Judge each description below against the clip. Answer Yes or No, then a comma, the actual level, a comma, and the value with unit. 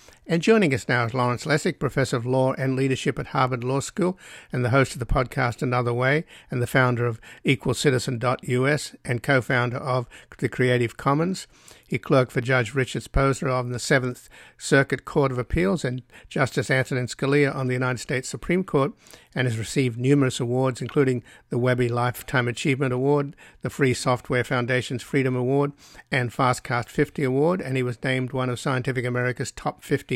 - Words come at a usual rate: Yes, average, 175 wpm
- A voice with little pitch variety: Yes, narrow, 2.0 semitones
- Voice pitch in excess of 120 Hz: Yes, low, 130 Hz